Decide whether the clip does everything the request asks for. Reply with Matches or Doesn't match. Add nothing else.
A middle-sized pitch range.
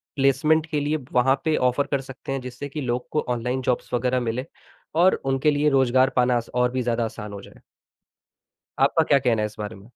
Doesn't match